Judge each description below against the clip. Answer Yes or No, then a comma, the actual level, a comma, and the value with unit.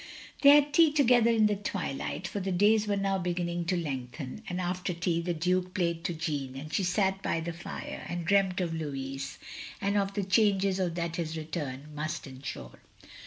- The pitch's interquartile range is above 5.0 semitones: No, average, 3.7 semitones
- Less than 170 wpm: No, average, 195 wpm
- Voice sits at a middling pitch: Yes, medium, 175 Hz